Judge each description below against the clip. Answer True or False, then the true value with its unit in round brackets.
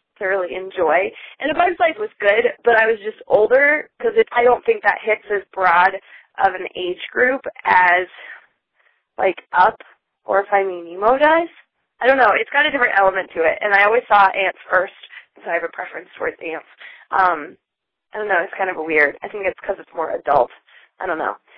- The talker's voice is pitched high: True (215 Hz)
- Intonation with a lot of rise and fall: True (7.3 semitones)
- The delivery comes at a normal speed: False (210 wpm)